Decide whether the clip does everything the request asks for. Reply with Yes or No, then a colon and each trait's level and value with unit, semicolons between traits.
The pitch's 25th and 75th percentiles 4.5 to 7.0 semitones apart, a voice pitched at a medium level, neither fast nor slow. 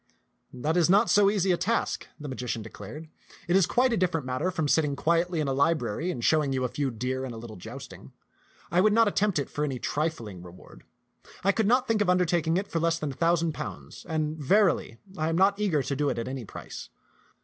No: wide, 5.6 semitones; medium, 160 Hz; fast, 235 wpm